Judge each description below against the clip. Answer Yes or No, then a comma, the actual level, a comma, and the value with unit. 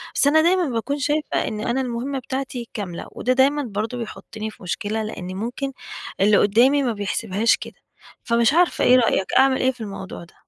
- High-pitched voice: Yes, high, 235 Hz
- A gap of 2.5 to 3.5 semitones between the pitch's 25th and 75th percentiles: No, average, 4.1 semitones